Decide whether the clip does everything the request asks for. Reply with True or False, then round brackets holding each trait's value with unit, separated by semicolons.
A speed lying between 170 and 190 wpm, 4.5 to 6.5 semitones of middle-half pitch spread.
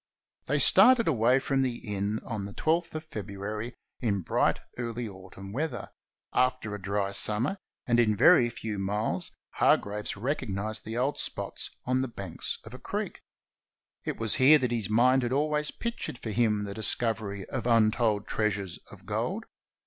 False (175 wpm; 3.9 semitones)